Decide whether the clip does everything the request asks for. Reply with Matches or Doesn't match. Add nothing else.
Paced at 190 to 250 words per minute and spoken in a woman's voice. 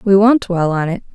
Doesn't match